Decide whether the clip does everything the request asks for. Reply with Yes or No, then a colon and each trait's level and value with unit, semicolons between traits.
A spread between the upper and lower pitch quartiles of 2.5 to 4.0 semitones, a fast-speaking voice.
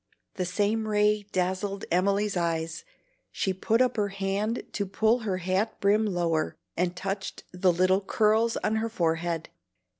No: average, 2.8 semitones; average, 150 wpm